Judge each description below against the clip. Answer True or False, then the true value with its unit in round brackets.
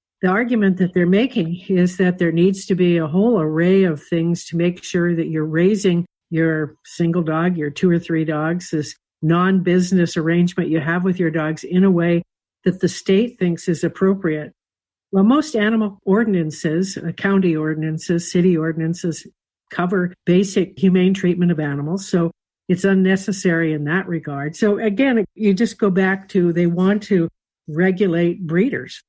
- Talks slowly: False (165 wpm)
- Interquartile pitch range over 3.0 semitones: False (2.5 semitones)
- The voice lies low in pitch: False (180 Hz)